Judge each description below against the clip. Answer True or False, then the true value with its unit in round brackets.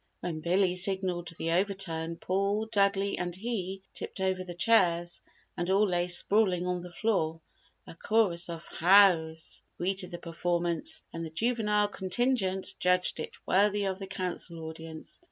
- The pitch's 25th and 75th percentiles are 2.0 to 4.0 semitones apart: True (2.5 semitones)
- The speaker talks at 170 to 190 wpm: False (150 wpm)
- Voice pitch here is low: False (185 Hz)